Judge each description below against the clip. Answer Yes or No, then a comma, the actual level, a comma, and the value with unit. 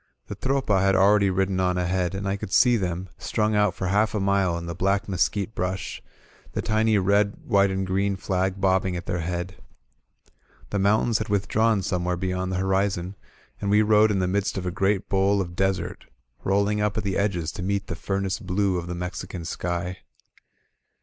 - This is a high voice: No, very low, 95 Hz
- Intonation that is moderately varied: No, narrow, 1.8 semitones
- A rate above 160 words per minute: Yes, average, 200 wpm